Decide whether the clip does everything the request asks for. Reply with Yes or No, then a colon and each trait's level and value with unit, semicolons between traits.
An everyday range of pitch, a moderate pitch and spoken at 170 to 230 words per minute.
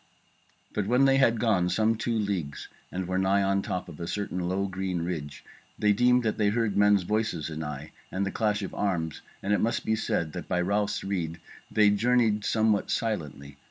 No: average, 3.5 semitones; low, 100 Hz; average, 195 wpm